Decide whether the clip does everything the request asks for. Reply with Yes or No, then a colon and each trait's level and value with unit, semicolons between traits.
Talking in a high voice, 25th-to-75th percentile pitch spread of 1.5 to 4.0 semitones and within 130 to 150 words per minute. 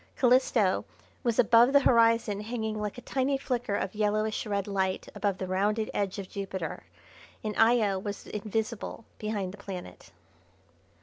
Yes: high, 215 Hz; narrow, 2.6 semitones; average, 145 wpm